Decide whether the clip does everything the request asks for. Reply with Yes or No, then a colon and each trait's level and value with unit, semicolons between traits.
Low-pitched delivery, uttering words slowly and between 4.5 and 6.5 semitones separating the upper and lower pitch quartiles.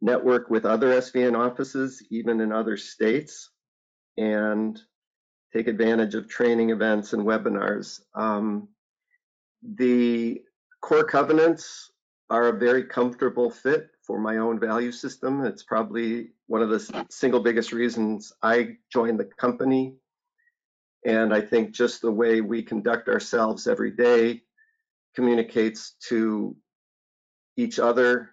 No: low, 120 Hz; slow, 125 wpm; narrow, 2.4 semitones